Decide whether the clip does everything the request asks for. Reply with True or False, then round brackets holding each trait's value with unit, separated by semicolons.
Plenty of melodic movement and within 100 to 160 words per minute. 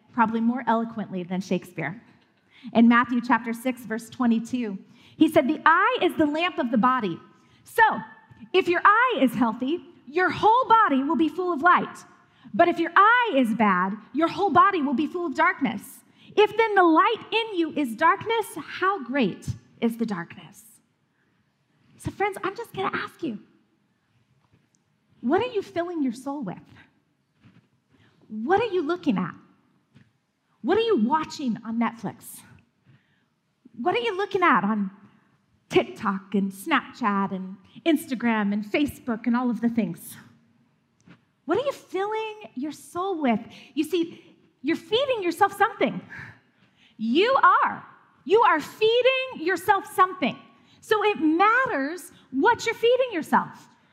True (8.7 semitones; 150 wpm)